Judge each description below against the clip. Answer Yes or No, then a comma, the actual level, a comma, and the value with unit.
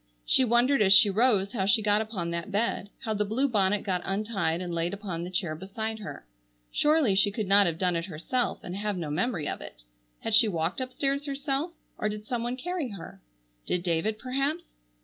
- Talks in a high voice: Yes, high, 210 Hz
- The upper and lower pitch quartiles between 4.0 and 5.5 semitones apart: Yes, average, 4.9 semitones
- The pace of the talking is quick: Yes, fast, 210 wpm